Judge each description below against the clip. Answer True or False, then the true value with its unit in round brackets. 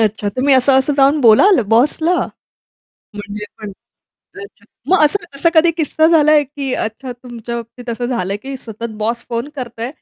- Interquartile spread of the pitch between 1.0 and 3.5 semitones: False (4.3 semitones)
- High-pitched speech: True (255 Hz)